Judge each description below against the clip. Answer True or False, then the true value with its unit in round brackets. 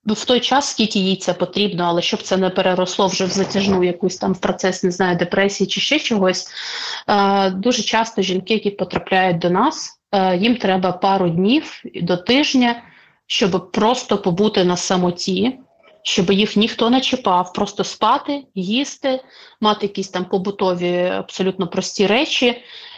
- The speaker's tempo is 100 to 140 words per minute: False (155 wpm)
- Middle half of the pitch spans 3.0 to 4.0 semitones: True (3.6 semitones)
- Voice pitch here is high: True (195 Hz)